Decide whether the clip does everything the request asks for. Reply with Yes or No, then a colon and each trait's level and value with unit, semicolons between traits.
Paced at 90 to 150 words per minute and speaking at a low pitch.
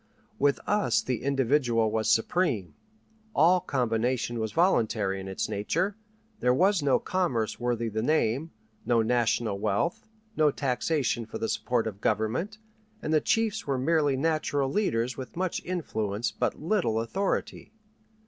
Yes: average, 140 wpm; low, 125 Hz